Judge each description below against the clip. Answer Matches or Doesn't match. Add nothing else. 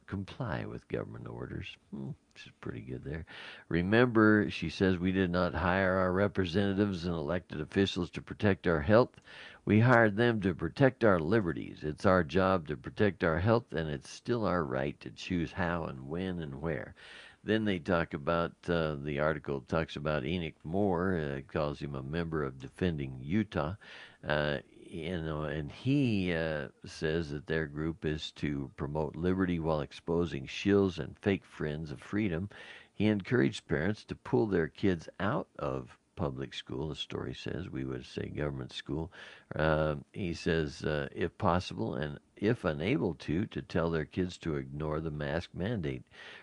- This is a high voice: Doesn't match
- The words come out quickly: Doesn't match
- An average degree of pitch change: Matches